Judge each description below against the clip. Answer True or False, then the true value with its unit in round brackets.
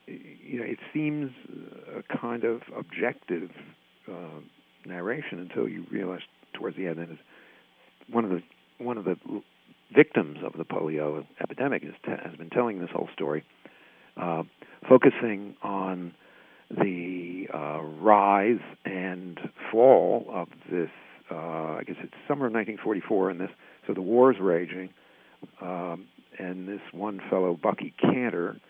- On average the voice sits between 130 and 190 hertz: False (90 Hz)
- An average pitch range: True (4.2 semitones)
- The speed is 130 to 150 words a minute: True (135 wpm)